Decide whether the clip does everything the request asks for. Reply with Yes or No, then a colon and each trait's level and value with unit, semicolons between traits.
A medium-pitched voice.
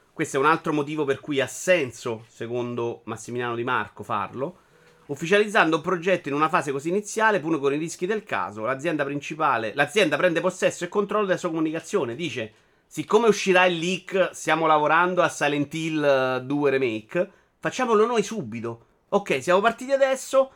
Yes: medium, 160 Hz